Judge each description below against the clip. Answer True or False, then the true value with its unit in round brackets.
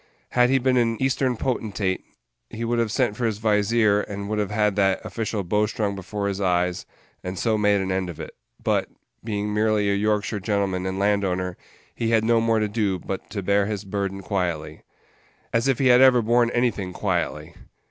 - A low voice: True (105 Hz)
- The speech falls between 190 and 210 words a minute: True (200 wpm)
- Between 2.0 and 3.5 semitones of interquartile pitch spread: True (2.8 semitones)